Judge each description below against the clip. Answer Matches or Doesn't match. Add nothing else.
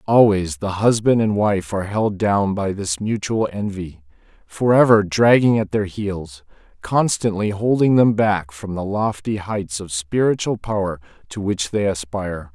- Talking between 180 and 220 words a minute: Doesn't match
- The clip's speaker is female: Doesn't match